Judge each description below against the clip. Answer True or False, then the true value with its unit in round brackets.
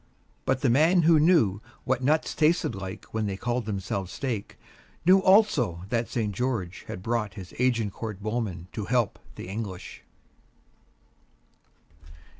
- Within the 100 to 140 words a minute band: True (135 wpm)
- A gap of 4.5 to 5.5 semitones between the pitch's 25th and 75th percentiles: True (5.1 semitones)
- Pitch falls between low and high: False (115 Hz)